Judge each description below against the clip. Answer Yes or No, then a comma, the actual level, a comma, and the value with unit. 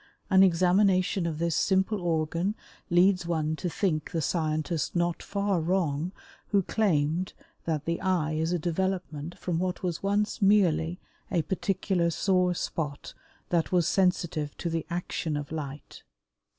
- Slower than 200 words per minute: Yes, average, 145 wpm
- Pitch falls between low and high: Yes, medium, 175 Hz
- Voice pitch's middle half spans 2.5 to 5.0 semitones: Yes, average, 2.9 semitones